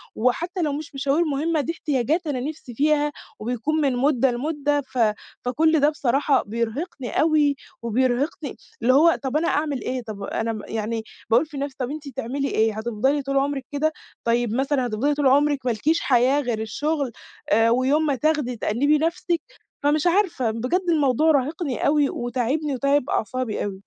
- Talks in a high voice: Yes, very high, 275 Hz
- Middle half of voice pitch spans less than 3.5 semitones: No, average, 3.8 semitones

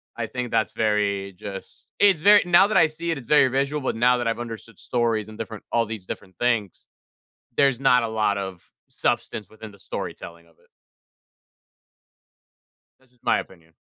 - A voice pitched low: Yes, low, 115 Hz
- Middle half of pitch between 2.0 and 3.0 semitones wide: No, average, 4.6 semitones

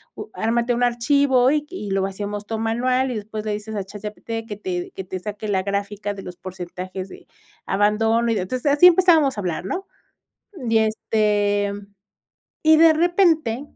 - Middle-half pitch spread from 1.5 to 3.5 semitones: No, average, 4.0 semitones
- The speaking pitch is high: Yes, high, 220 Hz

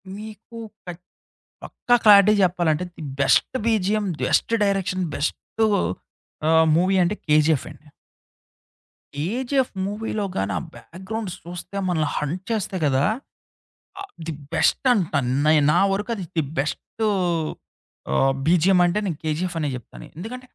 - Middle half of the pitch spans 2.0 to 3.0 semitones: No, average, 5.0 semitones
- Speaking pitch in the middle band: Yes, medium, 180 Hz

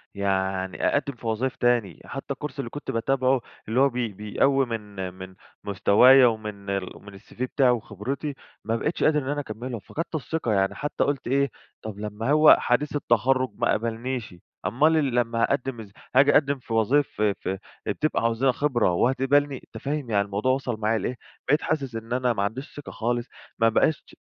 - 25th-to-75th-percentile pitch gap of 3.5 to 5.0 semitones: Yes, average, 4.2 semitones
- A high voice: No, low, 120 Hz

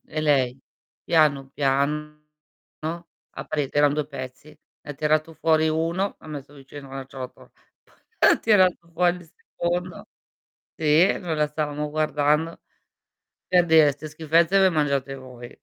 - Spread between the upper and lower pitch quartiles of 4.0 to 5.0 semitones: No, narrow, 2.5 semitones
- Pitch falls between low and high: Yes, medium, 150 Hz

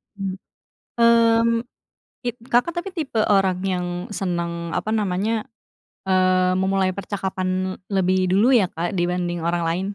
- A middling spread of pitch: Yes, average, 3.5 semitones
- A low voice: No, high, 190 Hz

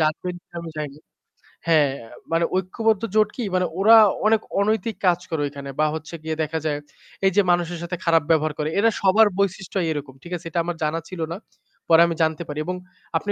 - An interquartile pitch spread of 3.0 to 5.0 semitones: Yes, average, 3.5 semitones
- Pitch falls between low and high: Yes, medium, 170 Hz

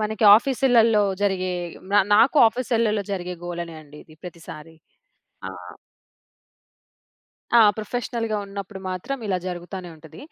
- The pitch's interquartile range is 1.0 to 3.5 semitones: No, average, 4.4 semitones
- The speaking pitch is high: Yes, high, 200 Hz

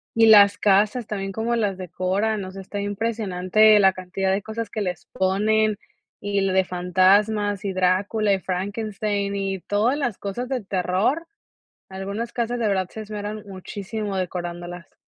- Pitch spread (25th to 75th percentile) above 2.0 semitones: Yes, narrow, 2.4 semitones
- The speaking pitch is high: Yes, high, 200 Hz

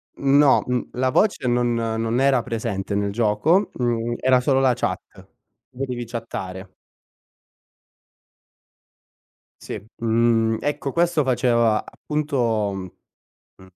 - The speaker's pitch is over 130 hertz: No, low, 120 Hz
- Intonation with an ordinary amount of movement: Yes, average, 3.0 semitones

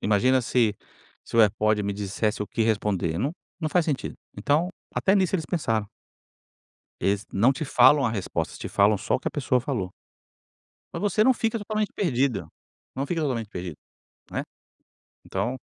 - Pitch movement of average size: No, wide, 7.0 semitones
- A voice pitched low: Yes, low, 125 Hz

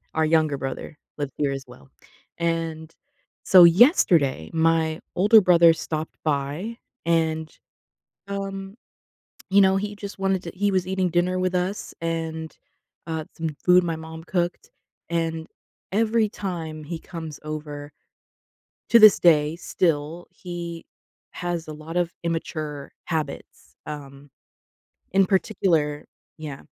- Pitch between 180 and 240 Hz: No, medium, 165 Hz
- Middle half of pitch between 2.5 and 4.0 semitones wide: Yes, average, 2.8 semitones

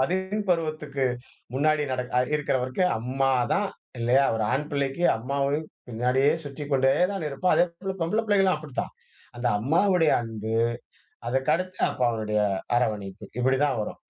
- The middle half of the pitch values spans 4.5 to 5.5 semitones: Yes, average, 4.8 semitones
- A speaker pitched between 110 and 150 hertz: Yes, medium, 140 Hz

